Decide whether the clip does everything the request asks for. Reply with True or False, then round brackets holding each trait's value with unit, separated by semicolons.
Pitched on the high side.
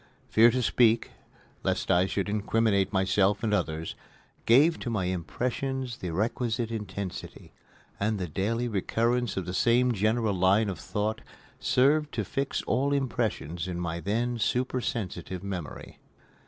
False (110 Hz)